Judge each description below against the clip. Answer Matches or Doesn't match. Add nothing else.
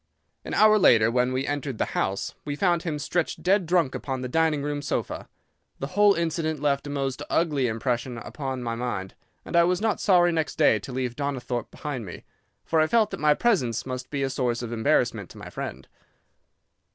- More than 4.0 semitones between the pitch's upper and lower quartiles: Matches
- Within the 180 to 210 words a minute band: Matches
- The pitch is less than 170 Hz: Matches